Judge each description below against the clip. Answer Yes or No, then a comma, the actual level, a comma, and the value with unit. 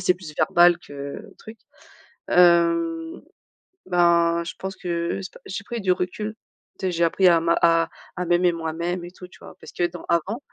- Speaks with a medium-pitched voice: Yes, medium, 175 Hz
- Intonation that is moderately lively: No, narrow, 1.4 semitones